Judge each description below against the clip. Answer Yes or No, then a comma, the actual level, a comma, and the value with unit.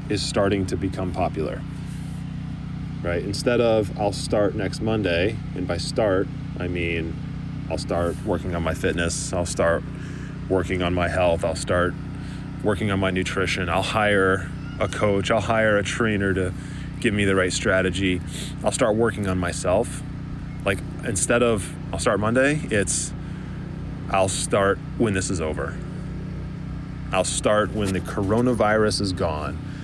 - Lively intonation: Yes, wide, 6.2 semitones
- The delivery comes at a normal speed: Yes, average, 150 wpm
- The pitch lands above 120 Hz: No, low, 100 Hz